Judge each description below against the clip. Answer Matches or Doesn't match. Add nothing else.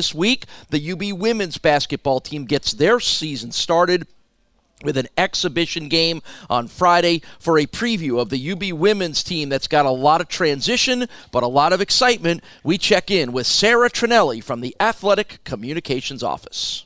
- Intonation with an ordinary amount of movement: Doesn't match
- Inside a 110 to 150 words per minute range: Doesn't match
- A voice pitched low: Doesn't match